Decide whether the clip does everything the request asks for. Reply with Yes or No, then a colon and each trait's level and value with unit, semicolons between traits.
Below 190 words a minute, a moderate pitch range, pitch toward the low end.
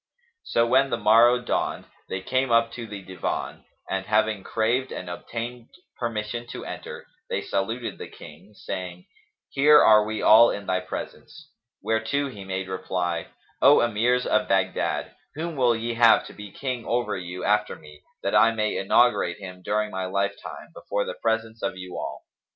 Yes: average, 170 wpm; average, 3.8 semitones; low, 110 Hz